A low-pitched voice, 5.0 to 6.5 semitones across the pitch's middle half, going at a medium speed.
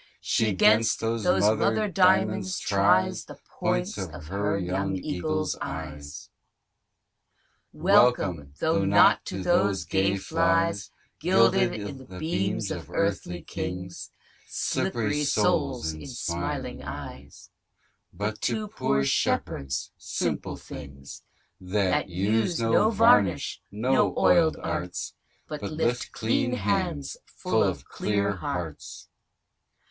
No: low, 100 Hz; wide, 5.5 semitones; slow, 105 wpm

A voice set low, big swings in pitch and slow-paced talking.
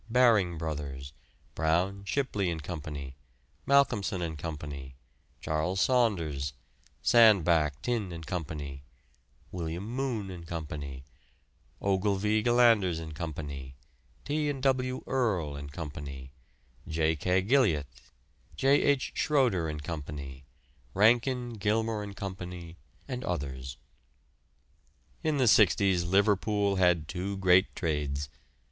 Yes: very low, 95 Hz; wide, 6.1 semitones; slow, 105 wpm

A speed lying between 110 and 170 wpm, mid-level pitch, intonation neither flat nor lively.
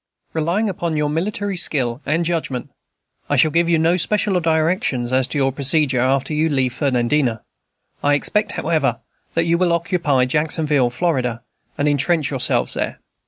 Yes: average, 160 wpm; medium, 150 Hz; average, 4.2 semitones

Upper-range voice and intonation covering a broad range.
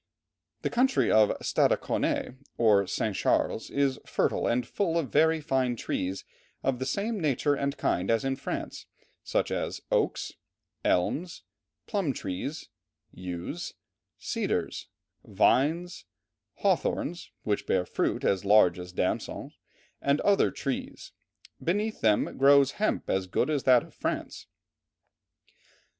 No: low, 135 Hz; wide, 7.7 semitones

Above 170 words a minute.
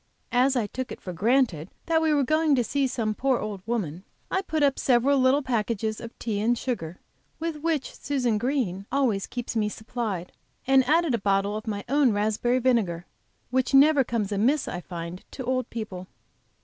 Yes: average, 190 wpm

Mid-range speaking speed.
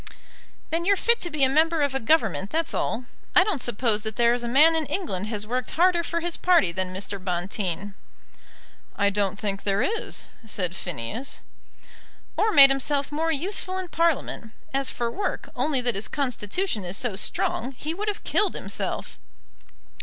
Yes: average, 180 wpm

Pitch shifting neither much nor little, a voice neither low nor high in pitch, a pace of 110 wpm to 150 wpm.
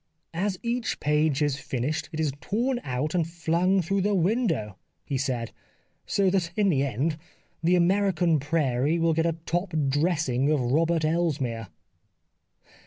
No: average, 4.2 semitones; medium, 160 Hz; average, 160 wpm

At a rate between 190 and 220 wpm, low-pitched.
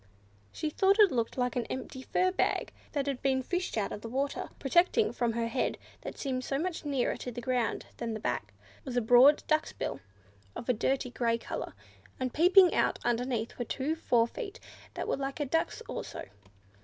No: average, 195 wpm; very high, 260 Hz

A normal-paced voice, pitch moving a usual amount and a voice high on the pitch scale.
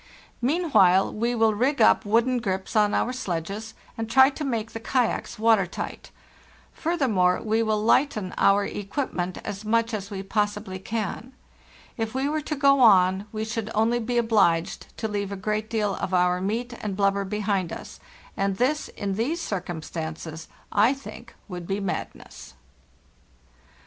Yes: average, 160 wpm; average, 3.4 semitones; high, 215 Hz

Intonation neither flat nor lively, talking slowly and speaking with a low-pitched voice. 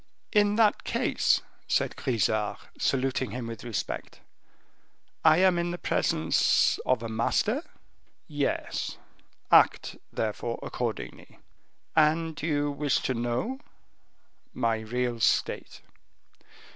No: wide, 5.8 semitones; slow, 105 wpm; low, 130 Hz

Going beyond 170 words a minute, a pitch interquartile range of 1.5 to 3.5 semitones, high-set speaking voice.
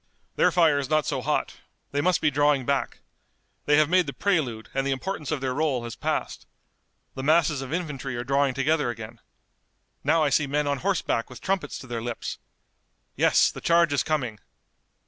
No: average, 190 wpm; average, 3.2 semitones; medium, 145 Hz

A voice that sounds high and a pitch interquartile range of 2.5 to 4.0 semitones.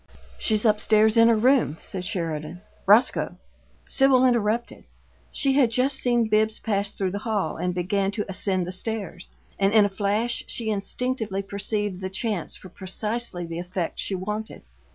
Yes: high, 210 Hz; average, 3.3 semitones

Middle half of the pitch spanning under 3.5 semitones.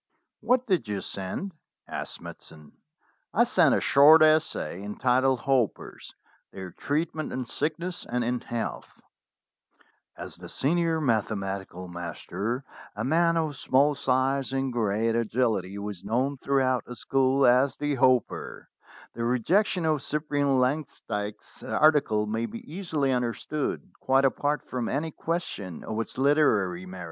No: average, 5.3 semitones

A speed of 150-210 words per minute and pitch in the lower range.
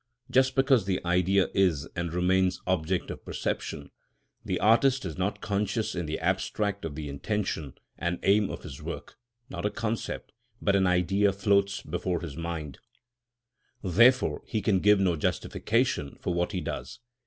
Yes: average, 160 wpm; very low, 95 Hz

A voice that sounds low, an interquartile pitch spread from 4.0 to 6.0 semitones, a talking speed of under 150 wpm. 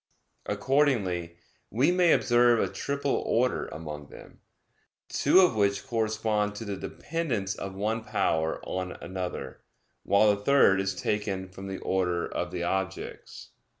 Yes: low, 100 Hz; average, 4.3 semitones; average, 140 wpm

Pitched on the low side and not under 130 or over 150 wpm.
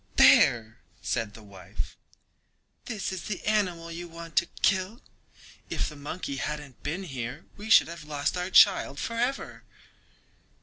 No: medium, 165 Hz; slow, 135 wpm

